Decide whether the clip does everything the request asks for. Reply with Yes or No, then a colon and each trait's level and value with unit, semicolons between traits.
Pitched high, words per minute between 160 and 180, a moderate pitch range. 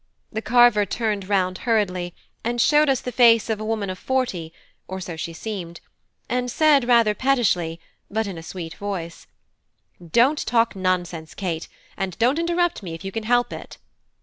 Yes: high, 210 Hz; average, 175 wpm; average, 4.9 semitones